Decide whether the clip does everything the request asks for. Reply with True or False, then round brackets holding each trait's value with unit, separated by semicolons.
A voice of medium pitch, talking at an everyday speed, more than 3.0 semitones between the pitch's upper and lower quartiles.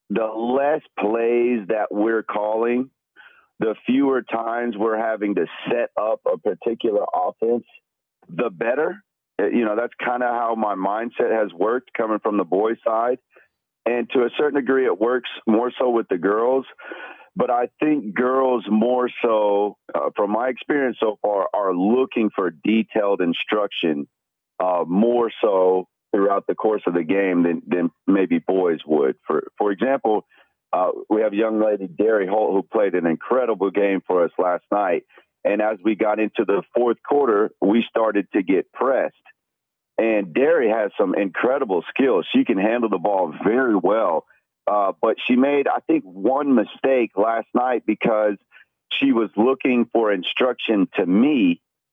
False (115 Hz; 160 wpm; 3.7 semitones)